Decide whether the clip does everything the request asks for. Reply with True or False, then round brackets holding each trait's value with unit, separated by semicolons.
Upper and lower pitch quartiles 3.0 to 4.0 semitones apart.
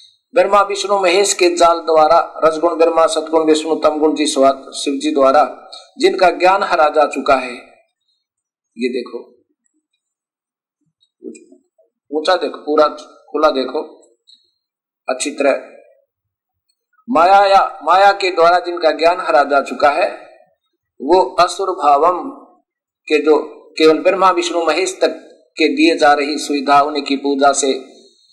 False (4.7 semitones)